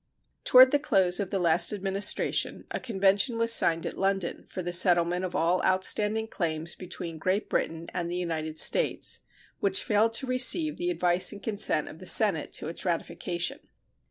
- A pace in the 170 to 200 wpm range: Yes, average, 175 wpm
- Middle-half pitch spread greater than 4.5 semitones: No, average, 3.8 semitones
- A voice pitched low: No, medium, 185 Hz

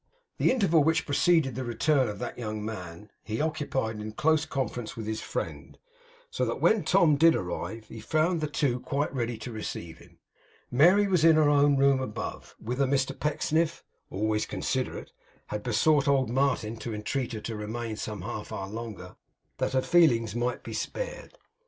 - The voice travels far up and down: Yes, wide, 5.8 semitones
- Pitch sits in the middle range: No, low, 130 Hz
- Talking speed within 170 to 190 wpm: Yes, average, 180 wpm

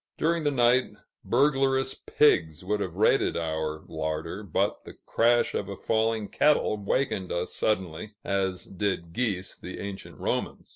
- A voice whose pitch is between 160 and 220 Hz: No, low, 100 Hz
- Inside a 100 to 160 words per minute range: Yes, average, 145 wpm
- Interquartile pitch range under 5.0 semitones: No, wide, 5.4 semitones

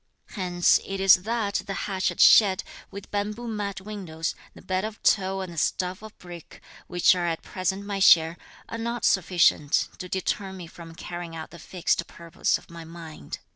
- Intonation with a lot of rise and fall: No, average, 2.8 semitones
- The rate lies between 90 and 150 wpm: No, average, 180 wpm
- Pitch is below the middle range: No, medium, 185 Hz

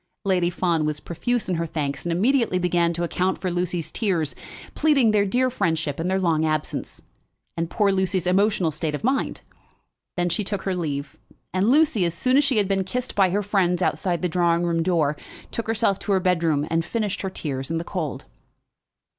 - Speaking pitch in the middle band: Yes, medium, 180 Hz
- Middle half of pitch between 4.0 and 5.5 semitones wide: No, average, 3.4 semitones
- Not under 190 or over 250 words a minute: Yes, average, 200 wpm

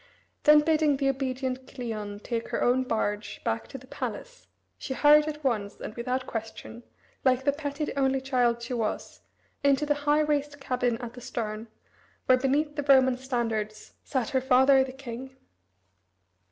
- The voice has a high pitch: Yes, very high, 260 Hz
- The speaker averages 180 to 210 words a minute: No, average, 165 wpm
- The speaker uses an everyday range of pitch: Yes, average, 3.0 semitones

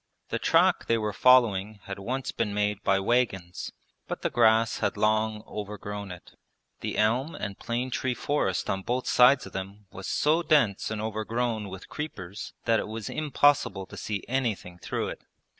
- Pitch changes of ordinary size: Yes, average, 3.7 semitones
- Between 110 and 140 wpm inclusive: No, average, 175 wpm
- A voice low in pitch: Yes, low, 110 Hz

